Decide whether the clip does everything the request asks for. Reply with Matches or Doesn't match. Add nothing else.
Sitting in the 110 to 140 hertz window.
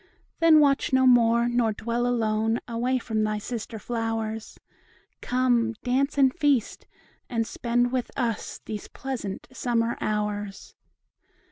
Doesn't match